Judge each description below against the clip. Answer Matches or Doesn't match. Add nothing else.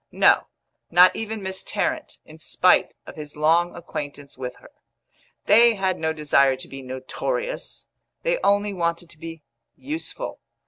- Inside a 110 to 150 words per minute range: Matches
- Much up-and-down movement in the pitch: Matches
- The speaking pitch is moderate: Matches